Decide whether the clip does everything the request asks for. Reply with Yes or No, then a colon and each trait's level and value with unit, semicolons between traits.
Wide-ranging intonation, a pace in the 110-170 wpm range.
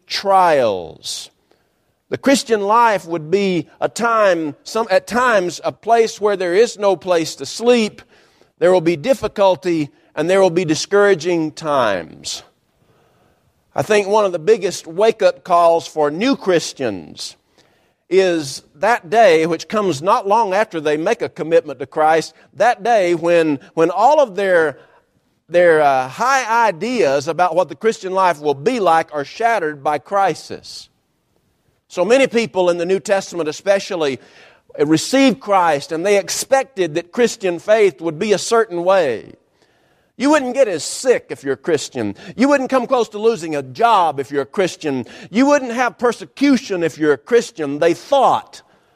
Yes: wide, 5.9 semitones; average, 160 wpm